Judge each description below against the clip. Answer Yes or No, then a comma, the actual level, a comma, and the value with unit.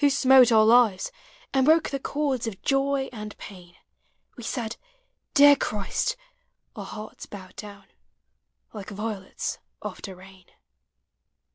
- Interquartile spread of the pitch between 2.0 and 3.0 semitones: No, average, 5.2 semitones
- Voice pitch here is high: Yes, high, 225 Hz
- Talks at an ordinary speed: No, slow, 125 wpm